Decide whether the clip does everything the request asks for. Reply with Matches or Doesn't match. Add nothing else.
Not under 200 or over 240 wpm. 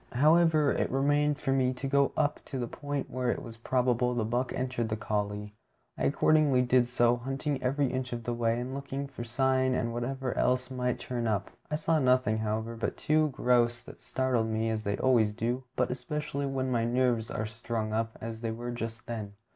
Matches